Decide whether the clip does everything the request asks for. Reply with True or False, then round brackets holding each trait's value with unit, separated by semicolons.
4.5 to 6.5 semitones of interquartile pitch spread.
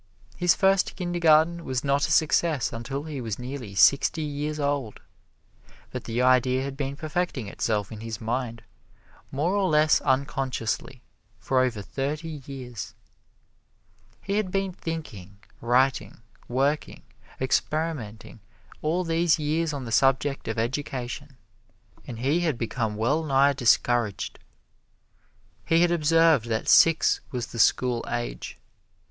True (4.8 semitones)